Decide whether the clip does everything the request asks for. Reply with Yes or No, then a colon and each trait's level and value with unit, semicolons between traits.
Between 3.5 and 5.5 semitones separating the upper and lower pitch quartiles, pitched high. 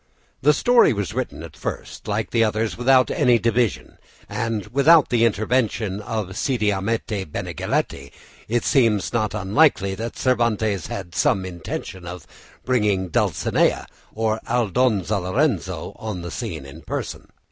No: average, 4.0 semitones; low, 110 Hz